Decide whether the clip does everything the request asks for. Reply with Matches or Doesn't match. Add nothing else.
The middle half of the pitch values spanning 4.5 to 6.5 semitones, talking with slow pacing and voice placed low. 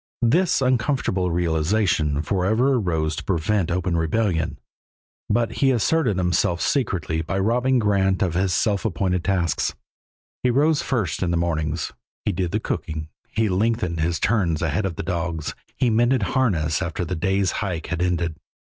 Doesn't match